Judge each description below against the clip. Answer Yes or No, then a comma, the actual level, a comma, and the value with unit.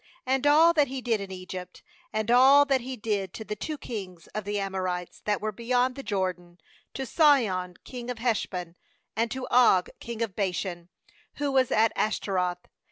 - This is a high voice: Yes, high, 215 Hz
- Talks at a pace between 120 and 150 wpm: No, average, 180 wpm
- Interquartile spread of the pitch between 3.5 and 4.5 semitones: No, wide, 5.4 semitones